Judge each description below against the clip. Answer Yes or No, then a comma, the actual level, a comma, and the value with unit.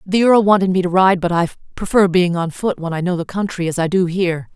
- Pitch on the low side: No, medium, 180 Hz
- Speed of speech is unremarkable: No, fast, 275 wpm